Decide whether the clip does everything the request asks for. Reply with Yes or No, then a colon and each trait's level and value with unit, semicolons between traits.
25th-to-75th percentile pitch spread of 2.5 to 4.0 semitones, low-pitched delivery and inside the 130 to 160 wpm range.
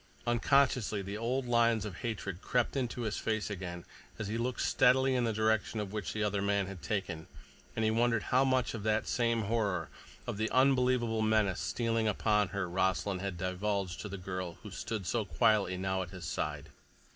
No: average, 3.4 semitones; low, 110 Hz; average, 180 wpm